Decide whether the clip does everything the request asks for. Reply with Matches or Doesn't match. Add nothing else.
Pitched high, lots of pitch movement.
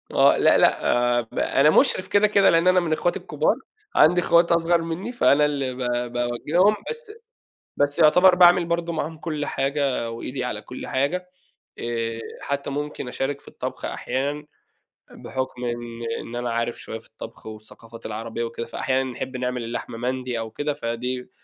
Doesn't match